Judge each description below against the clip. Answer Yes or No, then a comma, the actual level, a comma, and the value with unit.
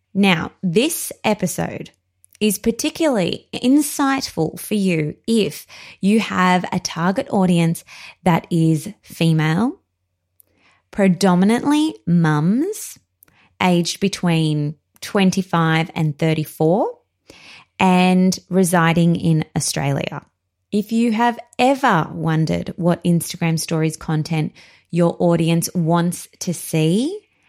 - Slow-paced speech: Yes, slow, 90 wpm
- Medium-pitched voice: Yes, medium, 175 Hz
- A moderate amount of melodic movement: Yes, average, 4.4 semitones